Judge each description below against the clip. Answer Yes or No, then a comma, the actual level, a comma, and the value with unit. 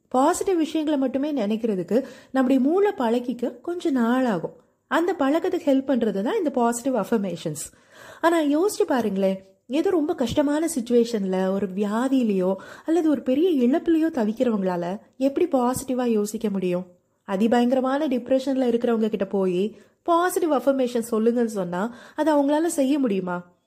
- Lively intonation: Yes, wide, 5.8 semitones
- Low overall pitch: No, very high, 255 Hz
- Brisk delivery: No, average, 120 wpm